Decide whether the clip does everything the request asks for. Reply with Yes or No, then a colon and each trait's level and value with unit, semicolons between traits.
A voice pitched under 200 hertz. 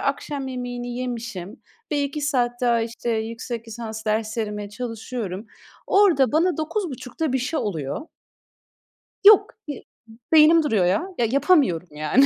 No: high, 245 Hz